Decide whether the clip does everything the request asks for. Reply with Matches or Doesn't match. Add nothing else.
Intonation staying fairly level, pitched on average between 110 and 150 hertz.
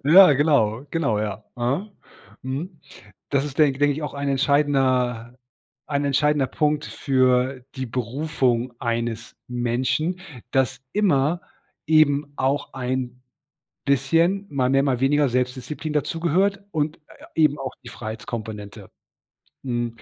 Doesn't match